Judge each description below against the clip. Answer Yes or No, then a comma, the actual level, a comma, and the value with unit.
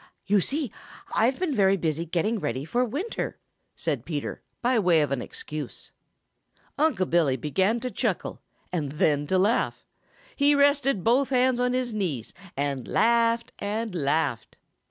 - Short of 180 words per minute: Yes, average, 150 wpm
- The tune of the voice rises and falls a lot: Yes, wide, 8.4 semitones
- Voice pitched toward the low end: No, high, 200 Hz